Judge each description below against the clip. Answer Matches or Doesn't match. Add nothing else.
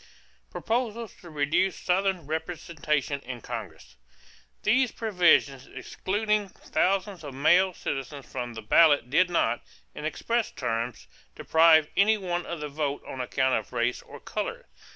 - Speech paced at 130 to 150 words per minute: Matches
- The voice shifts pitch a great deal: Matches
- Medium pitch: Matches